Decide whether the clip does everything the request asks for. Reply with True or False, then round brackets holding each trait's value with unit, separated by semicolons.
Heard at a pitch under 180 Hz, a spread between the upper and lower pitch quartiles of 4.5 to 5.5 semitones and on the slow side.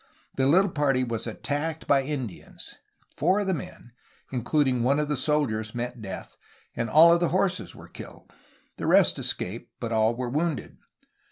False (135 Hz; 4.8 semitones; 170 wpm)